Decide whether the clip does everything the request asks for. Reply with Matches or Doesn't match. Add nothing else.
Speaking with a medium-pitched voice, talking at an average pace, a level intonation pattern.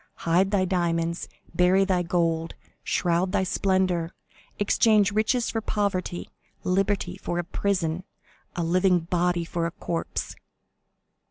Doesn't match